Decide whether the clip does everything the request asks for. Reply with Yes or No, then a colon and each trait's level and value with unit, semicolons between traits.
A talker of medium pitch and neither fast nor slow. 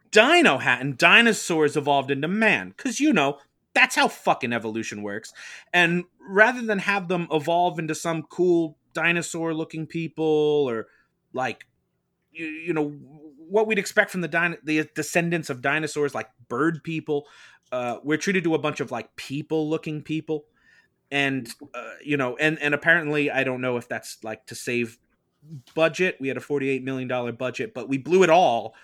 Yes: medium, 155 Hz; average, 170 wpm